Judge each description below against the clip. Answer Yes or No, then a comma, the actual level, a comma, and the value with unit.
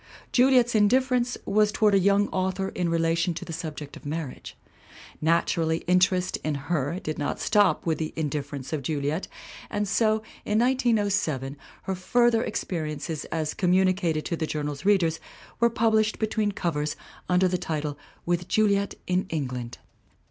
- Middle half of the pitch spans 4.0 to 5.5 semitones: Yes, average, 4.9 semitones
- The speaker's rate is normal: Yes, average, 150 wpm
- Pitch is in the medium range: Yes, medium, 180 Hz